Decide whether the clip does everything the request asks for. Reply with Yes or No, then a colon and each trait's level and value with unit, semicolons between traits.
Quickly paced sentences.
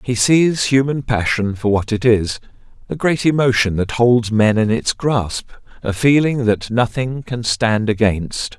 No: average, 170 wpm